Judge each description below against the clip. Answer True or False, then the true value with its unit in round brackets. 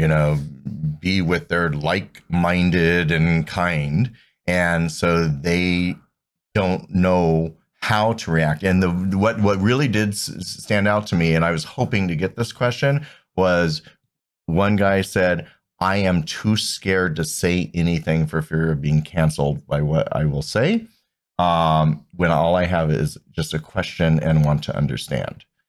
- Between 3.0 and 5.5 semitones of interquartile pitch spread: True (3.3 semitones)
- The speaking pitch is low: True (85 Hz)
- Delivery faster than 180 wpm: False (160 wpm)